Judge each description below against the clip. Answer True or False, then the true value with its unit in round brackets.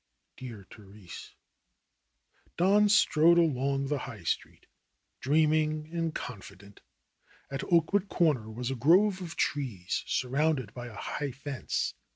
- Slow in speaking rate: True (130 wpm)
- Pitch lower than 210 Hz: True (140 Hz)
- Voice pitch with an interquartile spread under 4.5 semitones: False (5.2 semitones)